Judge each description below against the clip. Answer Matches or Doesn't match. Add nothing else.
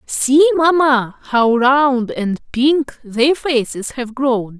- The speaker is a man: Doesn't match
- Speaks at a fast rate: Doesn't match